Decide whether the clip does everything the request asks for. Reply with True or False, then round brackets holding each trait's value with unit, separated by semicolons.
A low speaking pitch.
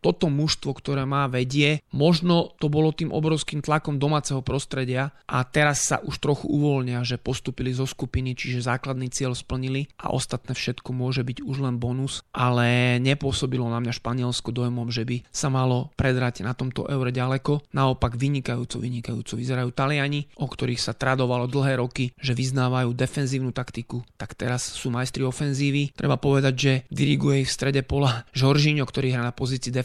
True (130 Hz)